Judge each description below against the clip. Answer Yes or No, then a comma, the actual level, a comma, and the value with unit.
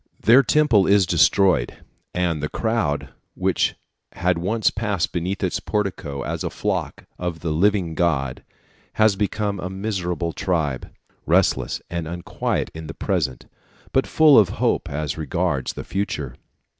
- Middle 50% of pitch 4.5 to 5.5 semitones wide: No, average, 4.1 semitones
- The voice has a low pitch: Yes, very low, 90 Hz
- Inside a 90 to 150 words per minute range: Yes, average, 145 wpm